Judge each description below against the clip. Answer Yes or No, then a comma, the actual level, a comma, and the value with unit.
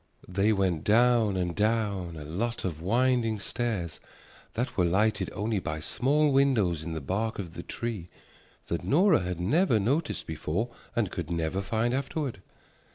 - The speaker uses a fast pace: No, average, 160 wpm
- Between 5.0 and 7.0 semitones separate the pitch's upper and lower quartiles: Yes, wide, 5.4 semitones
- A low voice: Yes, low, 105 Hz